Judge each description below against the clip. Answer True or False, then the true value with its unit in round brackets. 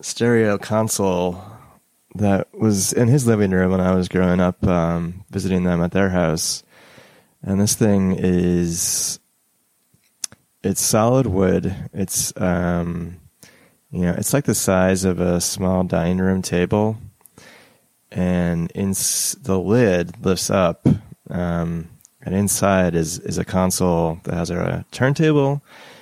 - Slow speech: True (130 wpm)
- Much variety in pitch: False (2.9 semitones)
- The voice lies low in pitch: True (95 Hz)